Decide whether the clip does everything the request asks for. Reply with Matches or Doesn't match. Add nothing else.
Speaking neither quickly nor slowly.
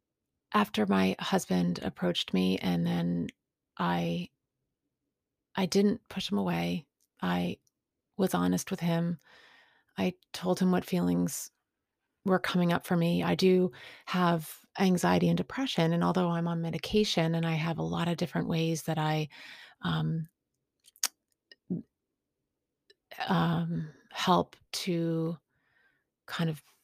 Doesn't match